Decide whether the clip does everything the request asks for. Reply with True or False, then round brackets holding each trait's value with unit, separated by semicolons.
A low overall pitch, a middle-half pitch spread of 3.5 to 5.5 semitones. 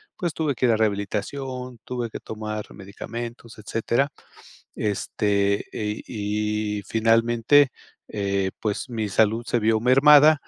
False (110 Hz; 3.1 semitones)